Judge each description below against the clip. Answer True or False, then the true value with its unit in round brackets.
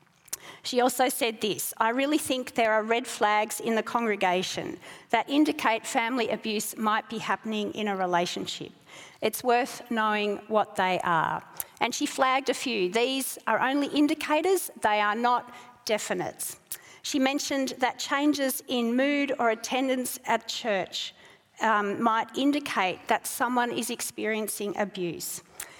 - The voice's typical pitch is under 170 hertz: False (230 Hz)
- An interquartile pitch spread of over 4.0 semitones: False (3.7 semitones)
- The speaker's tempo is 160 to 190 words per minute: False (140 wpm)